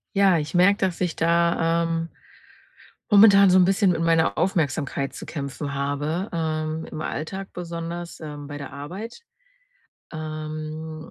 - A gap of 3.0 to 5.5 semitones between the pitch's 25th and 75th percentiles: No, narrow, 2.4 semitones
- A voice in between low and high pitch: Yes, medium, 165 Hz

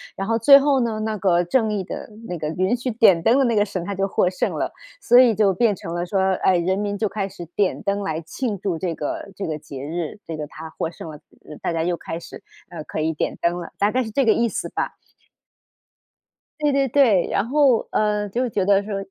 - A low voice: No, high, 200 Hz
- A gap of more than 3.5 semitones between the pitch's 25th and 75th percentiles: Yes, average, 4.7 semitones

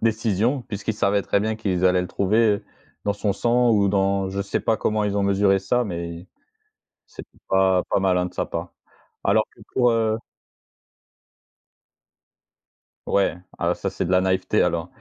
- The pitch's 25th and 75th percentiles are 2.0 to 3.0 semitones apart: Yes, narrow, 2.6 semitones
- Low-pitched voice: Yes, low, 100 Hz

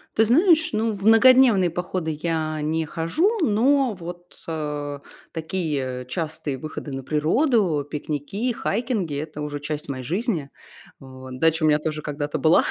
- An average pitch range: No, wide, 6.3 semitones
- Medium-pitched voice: Yes, medium, 160 Hz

